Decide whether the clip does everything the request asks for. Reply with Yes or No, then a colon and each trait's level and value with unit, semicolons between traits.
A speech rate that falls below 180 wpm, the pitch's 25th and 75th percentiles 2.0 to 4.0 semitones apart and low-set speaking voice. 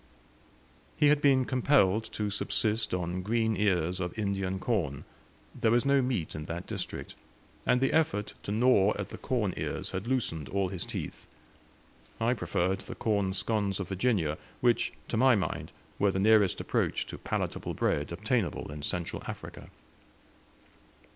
No: average, 155 wpm; average, 4.4 semitones; low, 100 Hz